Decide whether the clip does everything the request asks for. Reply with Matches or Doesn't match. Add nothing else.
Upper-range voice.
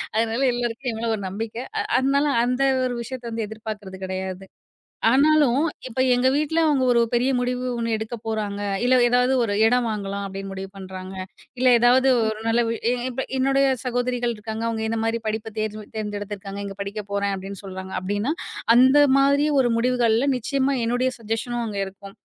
Matches